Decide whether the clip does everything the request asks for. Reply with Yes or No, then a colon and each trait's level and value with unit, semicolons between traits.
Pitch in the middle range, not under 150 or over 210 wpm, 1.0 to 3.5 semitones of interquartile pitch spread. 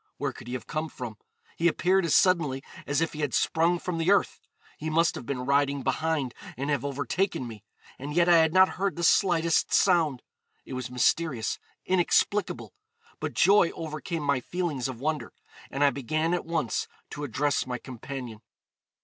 No: medium, 155 Hz; average, 180 wpm; average, 4.2 semitones